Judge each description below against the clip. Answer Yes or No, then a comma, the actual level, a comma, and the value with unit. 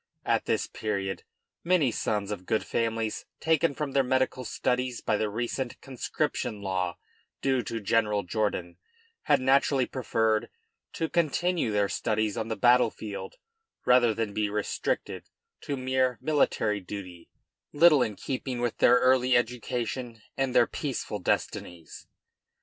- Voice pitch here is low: Yes, low, 120 Hz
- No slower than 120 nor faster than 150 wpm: Yes, average, 140 wpm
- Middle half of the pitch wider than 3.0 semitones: Yes, average, 3.7 semitones